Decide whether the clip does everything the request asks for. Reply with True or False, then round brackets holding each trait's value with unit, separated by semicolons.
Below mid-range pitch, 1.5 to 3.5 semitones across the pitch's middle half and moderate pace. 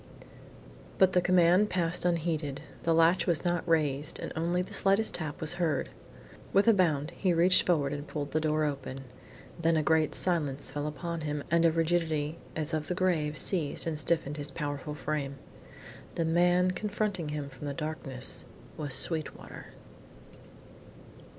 False (160 Hz; 2.9 semitones; 160 wpm)